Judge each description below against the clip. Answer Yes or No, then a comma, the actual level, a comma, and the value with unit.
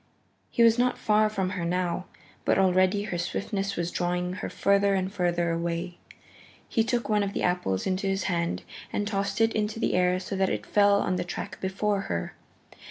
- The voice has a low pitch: No, high, 190 Hz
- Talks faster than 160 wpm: Yes, average, 195 wpm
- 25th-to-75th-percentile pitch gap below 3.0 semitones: Yes, narrow, 2.4 semitones